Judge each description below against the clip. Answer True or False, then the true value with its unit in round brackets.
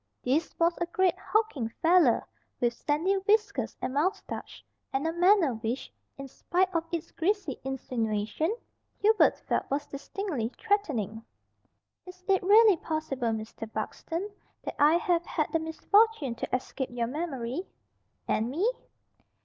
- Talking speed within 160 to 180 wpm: False (135 wpm)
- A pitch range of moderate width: False (6.6 semitones)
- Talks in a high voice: True (320 Hz)